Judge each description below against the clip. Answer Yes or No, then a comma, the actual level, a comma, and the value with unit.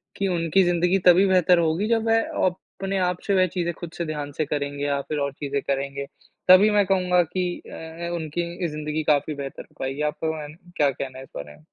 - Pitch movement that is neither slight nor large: Yes, average, 4.1 semitones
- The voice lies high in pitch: No, medium, 165 Hz